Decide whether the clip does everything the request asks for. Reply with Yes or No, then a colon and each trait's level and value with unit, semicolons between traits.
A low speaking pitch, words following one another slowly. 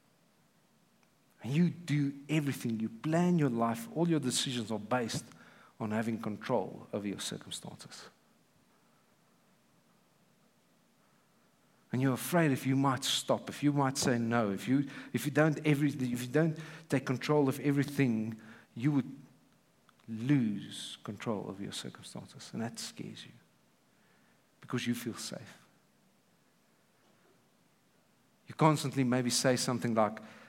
Yes: low, 130 Hz; slow, 125 wpm